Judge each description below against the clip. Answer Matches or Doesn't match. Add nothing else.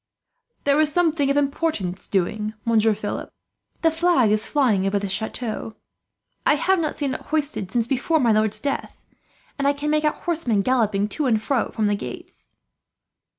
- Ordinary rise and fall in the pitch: Doesn't match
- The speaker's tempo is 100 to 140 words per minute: Doesn't match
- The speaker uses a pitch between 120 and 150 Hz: Doesn't match